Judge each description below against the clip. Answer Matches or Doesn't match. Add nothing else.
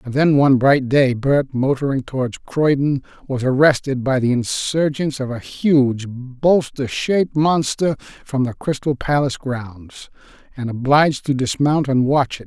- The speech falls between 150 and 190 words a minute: Matches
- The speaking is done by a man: Matches